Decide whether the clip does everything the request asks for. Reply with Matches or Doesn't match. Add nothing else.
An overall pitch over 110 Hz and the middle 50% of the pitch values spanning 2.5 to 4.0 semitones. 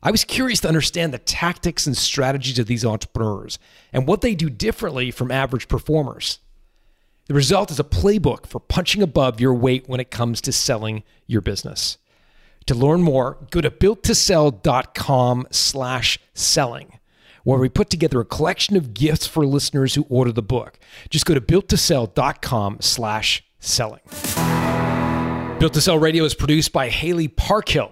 Doesn't match